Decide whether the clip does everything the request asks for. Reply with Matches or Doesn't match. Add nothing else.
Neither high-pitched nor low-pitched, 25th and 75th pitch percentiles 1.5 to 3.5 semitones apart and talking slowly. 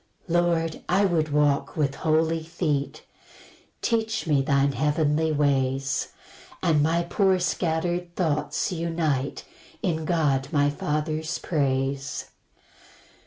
Matches